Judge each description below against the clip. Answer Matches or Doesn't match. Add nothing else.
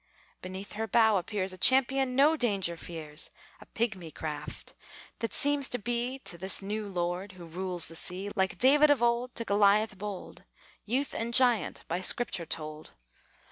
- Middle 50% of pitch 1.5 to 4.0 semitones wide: Doesn't match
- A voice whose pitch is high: Matches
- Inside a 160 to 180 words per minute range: Matches